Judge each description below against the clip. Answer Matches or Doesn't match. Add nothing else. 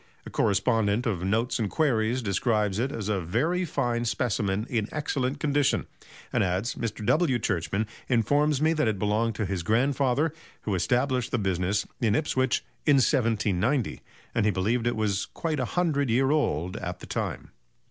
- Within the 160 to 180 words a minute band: Matches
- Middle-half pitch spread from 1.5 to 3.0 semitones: Doesn't match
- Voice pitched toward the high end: Doesn't match